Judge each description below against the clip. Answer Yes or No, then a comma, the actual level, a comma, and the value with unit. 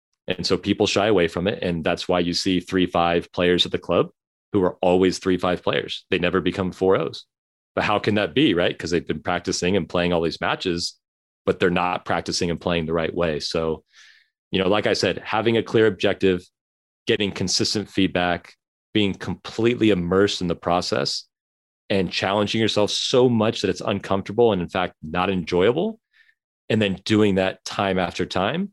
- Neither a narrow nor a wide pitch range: Yes, average, 3.0 semitones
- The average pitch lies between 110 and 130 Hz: No, very low, 95 Hz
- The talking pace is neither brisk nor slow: Yes, average, 190 wpm